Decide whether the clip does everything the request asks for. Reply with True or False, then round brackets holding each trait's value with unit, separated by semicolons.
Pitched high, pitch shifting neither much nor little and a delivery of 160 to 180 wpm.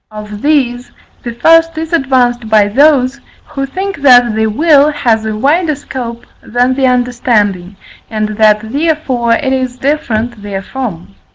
False (245 Hz; 4.5 semitones; 145 wpm)